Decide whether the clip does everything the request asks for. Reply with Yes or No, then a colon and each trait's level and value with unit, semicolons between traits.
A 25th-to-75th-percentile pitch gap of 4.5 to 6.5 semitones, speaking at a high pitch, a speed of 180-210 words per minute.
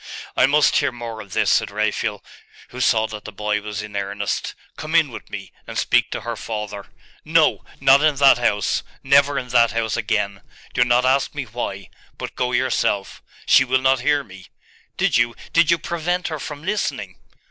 No: average, 5.0 semitones; low, 120 Hz; average, 190 wpm